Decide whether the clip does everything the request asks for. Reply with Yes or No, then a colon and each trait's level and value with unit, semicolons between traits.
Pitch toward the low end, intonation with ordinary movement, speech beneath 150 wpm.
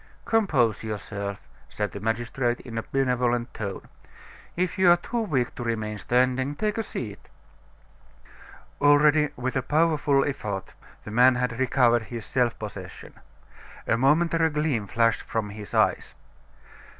Yes: low, 125 Hz; average, 4.6 semitones; average, 140 wpm